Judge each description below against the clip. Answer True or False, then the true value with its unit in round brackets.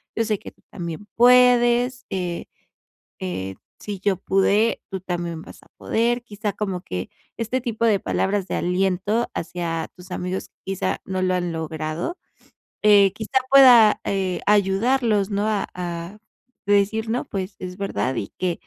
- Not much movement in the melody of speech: False (3.7 semitones)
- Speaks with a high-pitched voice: True (195 Hz)